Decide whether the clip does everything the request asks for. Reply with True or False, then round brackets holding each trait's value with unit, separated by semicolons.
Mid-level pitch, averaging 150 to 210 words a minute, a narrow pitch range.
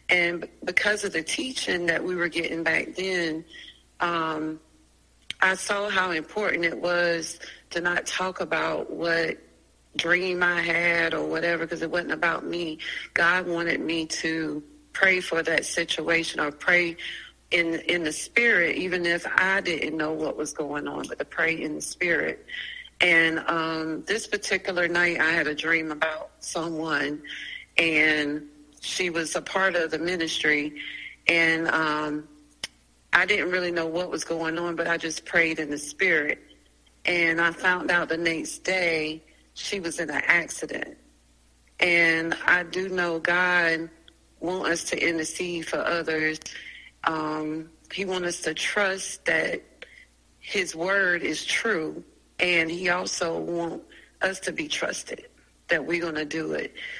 True (165 Hz; 155 wpm; 2.0 semitones)